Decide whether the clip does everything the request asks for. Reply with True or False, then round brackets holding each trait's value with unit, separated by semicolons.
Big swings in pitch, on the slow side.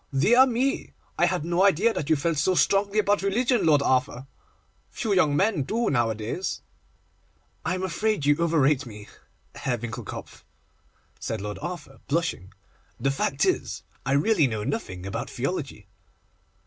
False (7.0 semitones; 150 wpm)